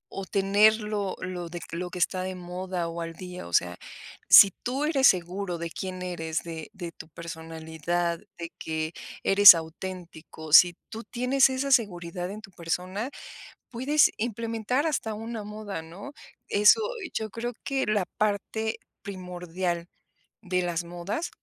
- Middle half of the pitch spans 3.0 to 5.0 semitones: Yes, average, 4.0 semitones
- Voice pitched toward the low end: No, medium, 185 Hz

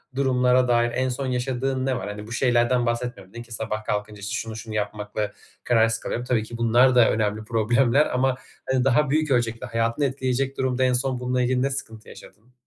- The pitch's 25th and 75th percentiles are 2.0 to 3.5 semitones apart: Yes, narrow, 2.5 semitones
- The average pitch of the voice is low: Yes, low, 120 Hz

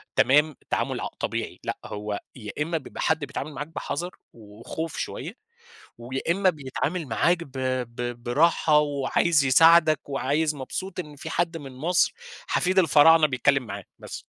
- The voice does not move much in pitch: No, average, 3.8 semitones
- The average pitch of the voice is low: No, medium, 150 Hz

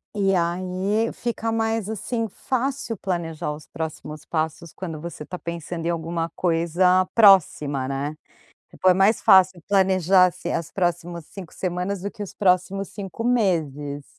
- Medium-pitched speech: Yes, medium, 180 Hz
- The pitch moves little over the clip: No, average, 3.2 semitones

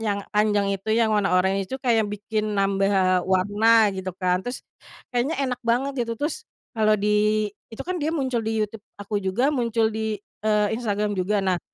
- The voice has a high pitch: Yes, high, 215 Hz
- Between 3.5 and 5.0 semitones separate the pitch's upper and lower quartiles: No, narrow, 2.6 semitones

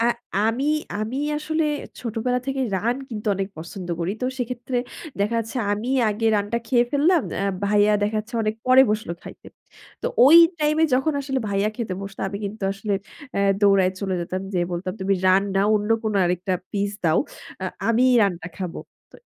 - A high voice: Yes, high, 210 Hz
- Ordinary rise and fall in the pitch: Yes, average, 4.1 semitones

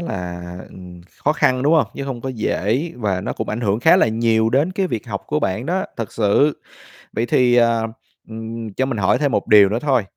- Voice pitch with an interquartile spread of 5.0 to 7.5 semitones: No, average, 4.3 semitones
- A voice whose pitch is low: Yes, low, 115 Hz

